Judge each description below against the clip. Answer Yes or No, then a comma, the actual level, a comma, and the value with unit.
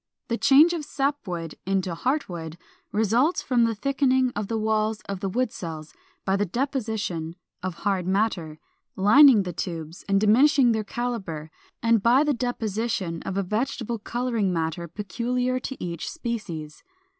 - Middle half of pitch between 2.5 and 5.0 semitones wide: No, wide, 5.5 semitones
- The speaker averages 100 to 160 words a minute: Yes, average, 155 wpm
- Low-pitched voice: No, high, 215 Hz